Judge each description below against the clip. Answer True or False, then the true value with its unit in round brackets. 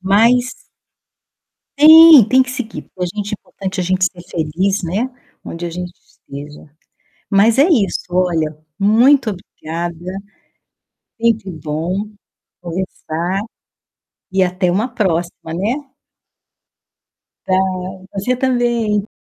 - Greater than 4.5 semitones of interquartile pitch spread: True (5.1 semitones)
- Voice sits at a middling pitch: False (195 Hz)